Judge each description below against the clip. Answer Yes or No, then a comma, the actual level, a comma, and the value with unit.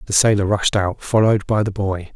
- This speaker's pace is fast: Yes, fast, 225 wpm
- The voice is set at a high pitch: No, low, 100 Hz